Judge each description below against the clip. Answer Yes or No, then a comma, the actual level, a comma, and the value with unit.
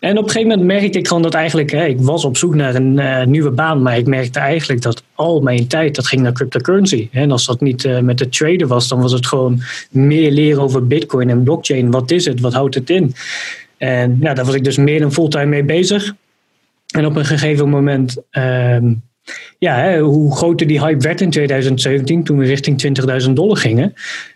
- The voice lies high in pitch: No, medium, 140 Hz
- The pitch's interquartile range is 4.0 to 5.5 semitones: No, average, 3.5 semitones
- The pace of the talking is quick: Yes, fast, 225 wpm